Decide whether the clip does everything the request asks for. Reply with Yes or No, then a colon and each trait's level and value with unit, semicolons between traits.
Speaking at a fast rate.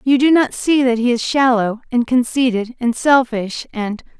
No: average, 185 wpm